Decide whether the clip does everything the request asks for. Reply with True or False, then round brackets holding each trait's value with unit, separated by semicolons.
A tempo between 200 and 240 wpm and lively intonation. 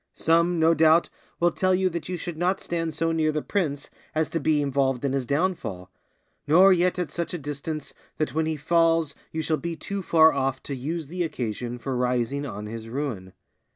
False (205 wpm; 3.7 semitones)